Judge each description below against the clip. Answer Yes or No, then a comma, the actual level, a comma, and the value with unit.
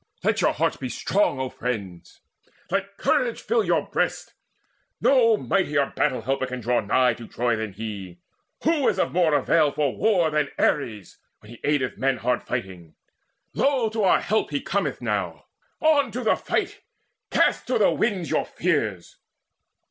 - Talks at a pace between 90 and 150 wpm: No, average, 165 wpm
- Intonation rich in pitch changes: Yes, wide, 9.0 semitones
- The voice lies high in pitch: No, medium, 145 Hz